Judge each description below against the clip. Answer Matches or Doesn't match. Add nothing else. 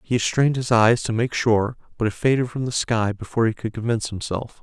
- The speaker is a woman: Doesn't match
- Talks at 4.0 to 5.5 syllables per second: Doesn't match